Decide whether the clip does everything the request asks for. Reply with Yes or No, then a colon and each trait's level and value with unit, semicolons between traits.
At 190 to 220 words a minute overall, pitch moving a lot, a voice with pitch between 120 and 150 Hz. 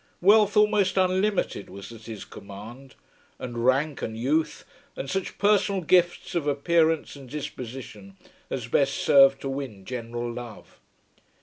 No: slow, 135 wpm; wide, 6.7 semitones; low, 135 Hz